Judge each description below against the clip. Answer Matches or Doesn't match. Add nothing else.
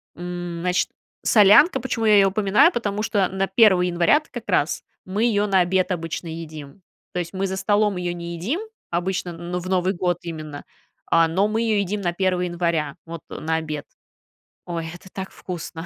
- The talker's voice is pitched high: Doesn't match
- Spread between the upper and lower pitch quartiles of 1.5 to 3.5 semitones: Matches